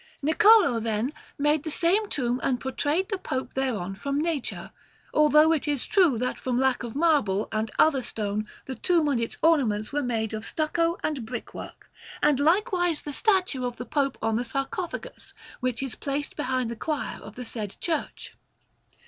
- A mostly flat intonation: No, average, 4.9 semitones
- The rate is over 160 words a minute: Yes, average, 180 wpm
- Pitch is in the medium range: No, very high, 275 Hz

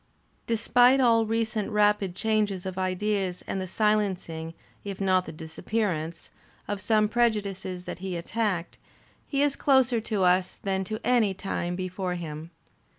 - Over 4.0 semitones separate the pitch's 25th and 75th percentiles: No, average, 3.3 semitones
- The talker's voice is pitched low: No, high, 195 Hz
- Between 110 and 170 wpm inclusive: Yes, average, 145 wpm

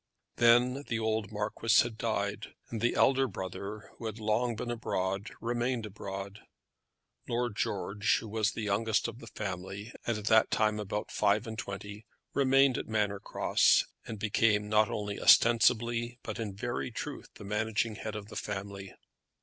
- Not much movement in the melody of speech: Yes, narrow, 2.3 semitones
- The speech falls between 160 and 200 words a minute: Yes, average, 165 wpm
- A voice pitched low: Yes, low, 110 Hz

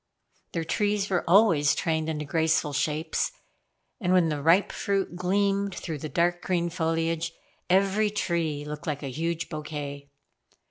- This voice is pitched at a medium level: Yes, medium, 165 Hz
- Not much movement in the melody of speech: No, average, 3.5 semitones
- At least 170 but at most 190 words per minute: No, average, 145 wpm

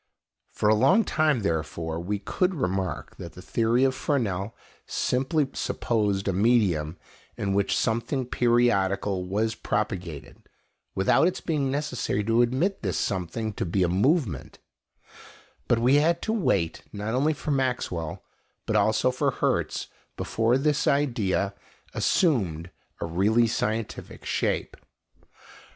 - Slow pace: Yes, slow, 130 wpm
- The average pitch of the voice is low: Yes, low, 110 Hz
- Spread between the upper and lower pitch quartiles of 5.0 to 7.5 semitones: Yes, wide, 5.5 semitones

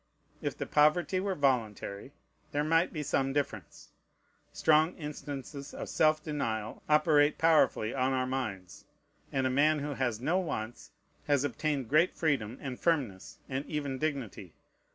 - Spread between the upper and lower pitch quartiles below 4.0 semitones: Yes, average, 3.3 semitones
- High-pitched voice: No, medium, 140 Hz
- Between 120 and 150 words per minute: Yes, average, 145 wpm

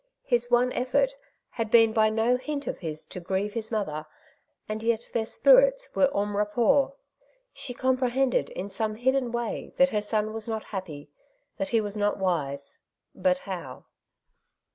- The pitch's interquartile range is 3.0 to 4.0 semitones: Yes, average, 3.7 semitones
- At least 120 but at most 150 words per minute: No, average, 165 wpm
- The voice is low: No, high, 225 Hz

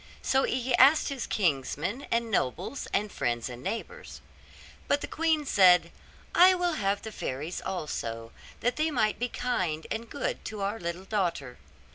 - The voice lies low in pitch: No, high, 210 Hz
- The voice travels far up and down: Yes, wide, 7.7 semitones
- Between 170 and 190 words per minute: No, average, 160 wpm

